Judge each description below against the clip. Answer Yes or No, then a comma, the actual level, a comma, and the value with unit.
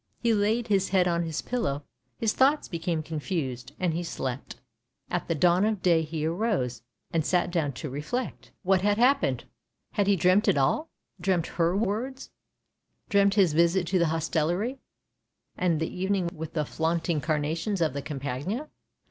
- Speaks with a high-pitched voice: No, medium, 175 Hz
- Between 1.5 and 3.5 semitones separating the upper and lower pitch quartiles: No, average, 4.3 semitones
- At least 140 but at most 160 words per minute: No, average, 180 wpm